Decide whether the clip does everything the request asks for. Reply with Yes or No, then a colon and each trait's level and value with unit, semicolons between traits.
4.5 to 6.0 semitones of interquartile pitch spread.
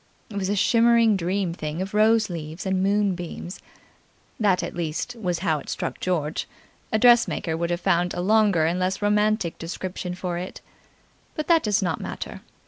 No: average, 3.4 semitones